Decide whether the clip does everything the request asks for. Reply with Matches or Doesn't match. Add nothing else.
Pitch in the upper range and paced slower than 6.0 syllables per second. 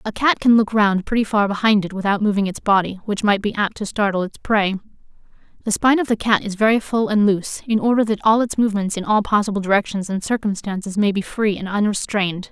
Doesn't match